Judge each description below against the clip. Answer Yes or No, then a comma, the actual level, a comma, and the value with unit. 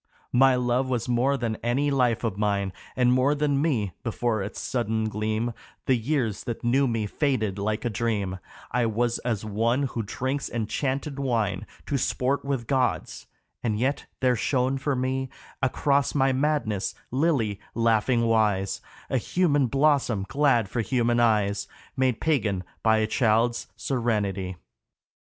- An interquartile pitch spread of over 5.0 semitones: No, average, 3.5 semitones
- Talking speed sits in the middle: Yes, average, 145 wpm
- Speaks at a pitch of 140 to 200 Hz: No, low, 120 Hz